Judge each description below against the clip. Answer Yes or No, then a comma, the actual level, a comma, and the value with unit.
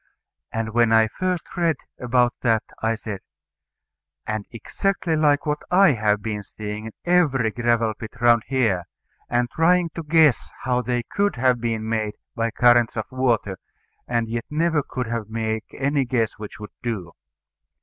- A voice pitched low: Yes, low, 120 Hz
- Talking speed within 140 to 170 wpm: Yes, average, 160 wpm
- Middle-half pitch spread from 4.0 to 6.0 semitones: Yes, average, 4.5 semitones